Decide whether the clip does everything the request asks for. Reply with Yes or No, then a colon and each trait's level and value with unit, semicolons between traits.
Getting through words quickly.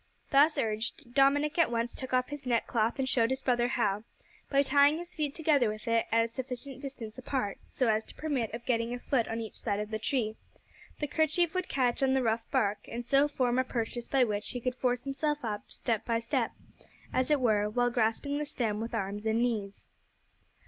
Yes: fast, 215 wpm